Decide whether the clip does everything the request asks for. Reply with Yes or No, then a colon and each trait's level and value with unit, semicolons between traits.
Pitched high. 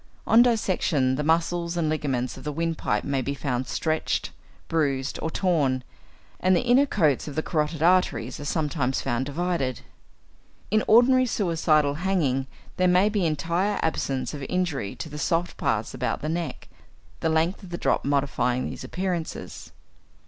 No: medium, 160 Hz